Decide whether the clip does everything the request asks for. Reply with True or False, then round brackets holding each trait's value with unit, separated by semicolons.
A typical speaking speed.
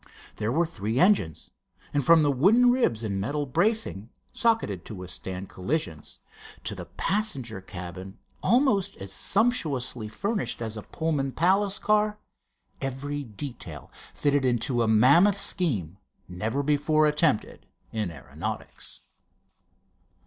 False (120 wpm)